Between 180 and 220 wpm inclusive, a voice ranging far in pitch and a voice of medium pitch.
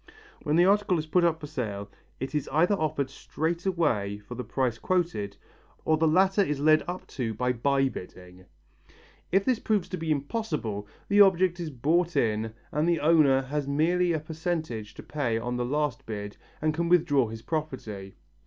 Yes: average, 190 wpm; wide, 5.9 semitones; medium, 150 Hz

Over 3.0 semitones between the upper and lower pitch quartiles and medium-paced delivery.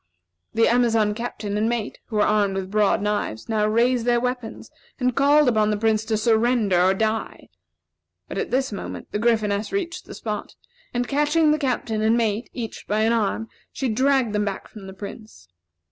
No: average, 2.7 semitones; average, 190 wpm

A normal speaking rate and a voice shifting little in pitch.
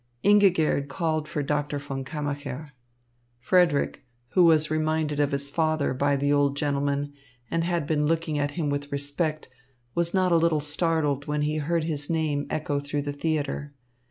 Yes: average, 165 wpm; narrow, 2.0 semitones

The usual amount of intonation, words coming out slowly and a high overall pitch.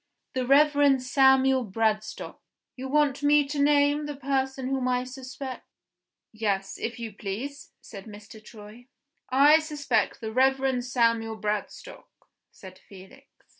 Yes: average, 4.0 semitones; slow, 130 wpm; very high, 260 Hz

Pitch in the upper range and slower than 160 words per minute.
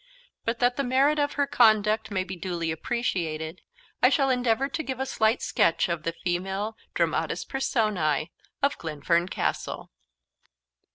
Yes: high, 215 Hz; average, 150 wpm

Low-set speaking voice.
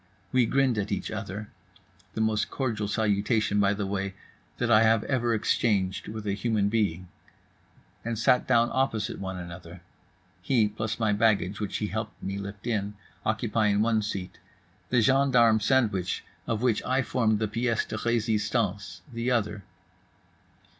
Yes: low, 110 Hz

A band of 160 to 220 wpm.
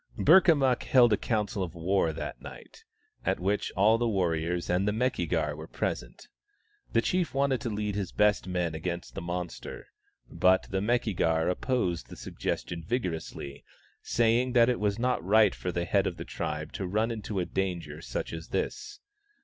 Yes: average, 180 wpm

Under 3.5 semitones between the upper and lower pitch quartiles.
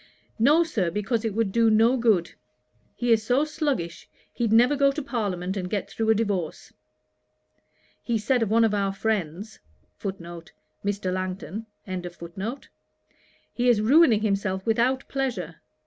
No: average, 4.0 semitones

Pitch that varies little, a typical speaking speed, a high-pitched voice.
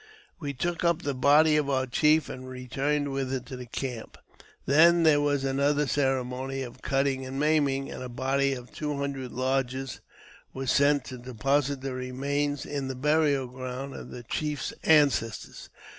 No: narrow, 2.0 semitones; average, 175 wpm; low, 135 Hz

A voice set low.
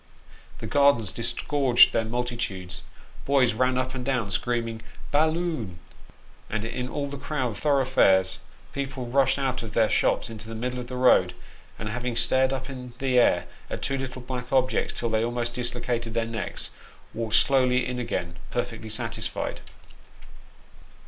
Yes: low, 125 Hz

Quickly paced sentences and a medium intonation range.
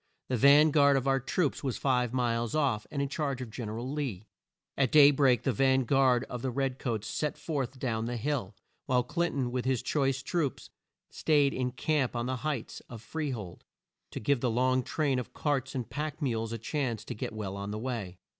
Yes: fast, 220 wpm; average, 3.0 semitones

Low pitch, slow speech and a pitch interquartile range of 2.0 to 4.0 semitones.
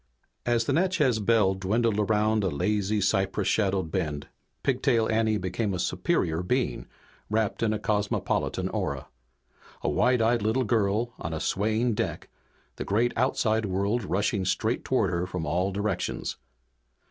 No: low, 105 Hz; average, 145 wpm; average, 3.1 semitones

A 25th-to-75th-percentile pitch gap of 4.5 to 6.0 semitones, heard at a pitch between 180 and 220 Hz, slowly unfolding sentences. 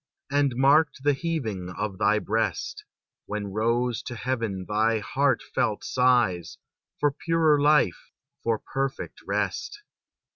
No: average, 5.1 semitones; low, 120 Hz; slow, 115 wpm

